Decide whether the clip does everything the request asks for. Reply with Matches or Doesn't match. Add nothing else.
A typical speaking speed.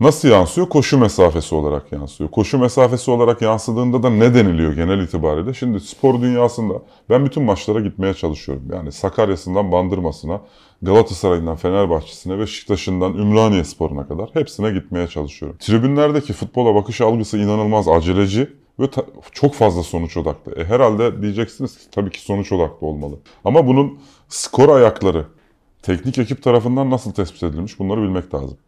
Doesn't match